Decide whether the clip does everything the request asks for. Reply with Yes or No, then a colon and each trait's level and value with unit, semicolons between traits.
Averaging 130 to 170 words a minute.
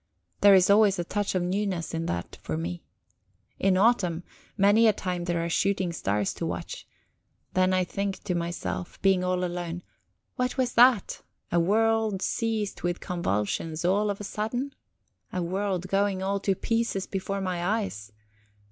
Yes: average, 165 wpm